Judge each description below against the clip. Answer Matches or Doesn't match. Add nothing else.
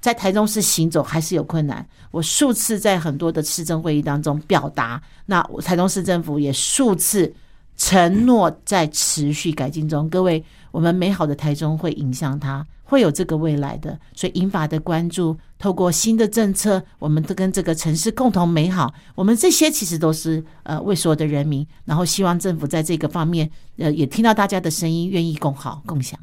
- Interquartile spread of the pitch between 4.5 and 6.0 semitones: Doesn't match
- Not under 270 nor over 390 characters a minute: Matches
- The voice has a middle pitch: Matches